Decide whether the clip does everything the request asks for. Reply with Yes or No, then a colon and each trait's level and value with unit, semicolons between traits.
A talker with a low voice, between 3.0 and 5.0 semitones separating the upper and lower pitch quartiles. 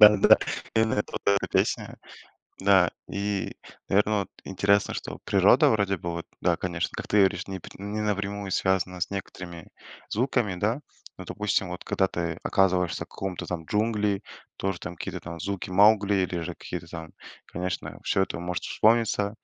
No: very low, 95 Hz; narrow, 2.4 semitones